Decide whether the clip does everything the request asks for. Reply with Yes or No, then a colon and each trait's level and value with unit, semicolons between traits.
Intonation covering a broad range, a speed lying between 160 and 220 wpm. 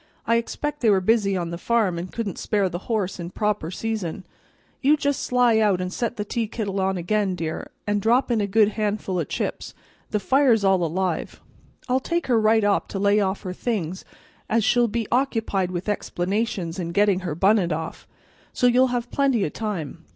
No: average, 3.9 semitones; average, 195 wpm